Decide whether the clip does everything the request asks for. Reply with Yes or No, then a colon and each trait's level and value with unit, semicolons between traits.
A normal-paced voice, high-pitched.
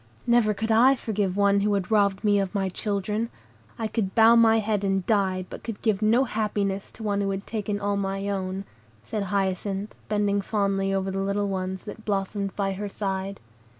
Yes: average, 195 wpm; high, 200 Hz